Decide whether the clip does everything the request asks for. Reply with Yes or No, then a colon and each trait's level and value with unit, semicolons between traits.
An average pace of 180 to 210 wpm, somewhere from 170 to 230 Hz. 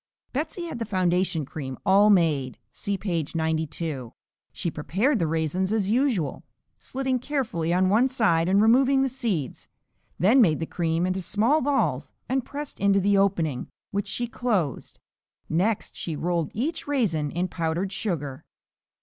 No: average, 150 wpm; high, 190 Hz